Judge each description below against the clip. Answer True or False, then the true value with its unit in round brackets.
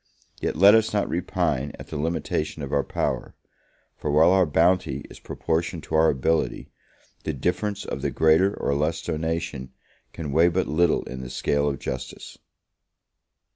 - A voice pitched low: True (80 Hz)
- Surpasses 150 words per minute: True (165 wpm)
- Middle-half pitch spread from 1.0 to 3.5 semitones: True (3.2 semitones)